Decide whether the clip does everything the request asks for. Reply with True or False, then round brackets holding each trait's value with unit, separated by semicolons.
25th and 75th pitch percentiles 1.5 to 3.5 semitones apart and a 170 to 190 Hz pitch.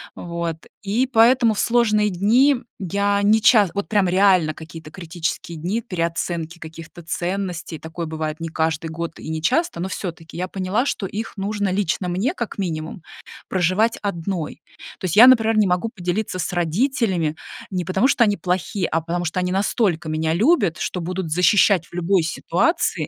False (4.0 semitones; 185 Hz)